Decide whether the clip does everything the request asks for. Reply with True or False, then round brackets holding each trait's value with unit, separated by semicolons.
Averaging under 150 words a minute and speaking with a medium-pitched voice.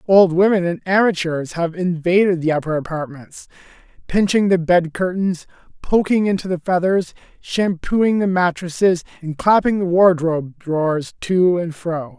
True (140 wpm; 175 Hz)